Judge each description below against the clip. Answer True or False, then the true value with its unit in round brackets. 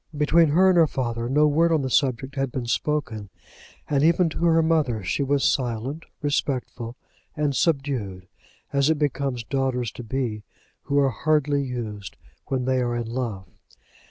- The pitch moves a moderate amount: True (3.9 semitones)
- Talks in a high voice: False (135 Hz)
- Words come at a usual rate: True (165 wpm)